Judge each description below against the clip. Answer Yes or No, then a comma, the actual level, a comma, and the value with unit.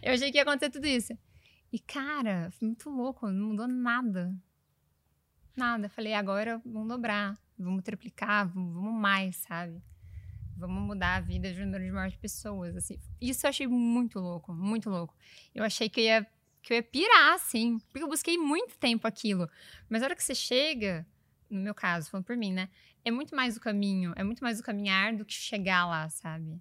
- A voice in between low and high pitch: No, high, 215 Hz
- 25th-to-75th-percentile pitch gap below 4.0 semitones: No, average, 4.5 semitones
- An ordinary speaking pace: No, fast, 195 wpm